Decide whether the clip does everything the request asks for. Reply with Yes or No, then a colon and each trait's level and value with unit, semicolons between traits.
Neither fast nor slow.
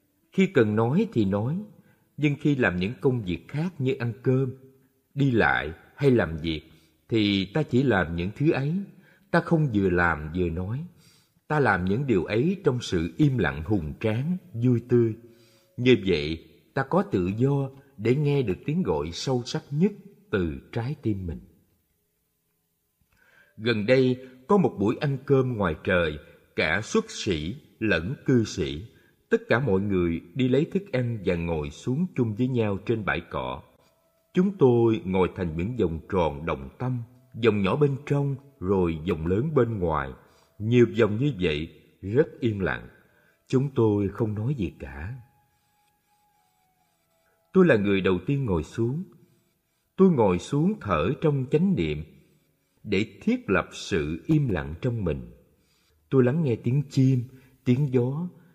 No: slow, 160 wpm